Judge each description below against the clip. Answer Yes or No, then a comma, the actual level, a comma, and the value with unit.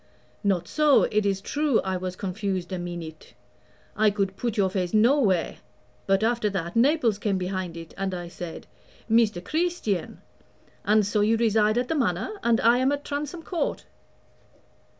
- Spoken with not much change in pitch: No, average, 4.3 semitones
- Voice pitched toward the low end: No, high, 210 Hz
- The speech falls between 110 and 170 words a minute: Yes, average, 165 wpm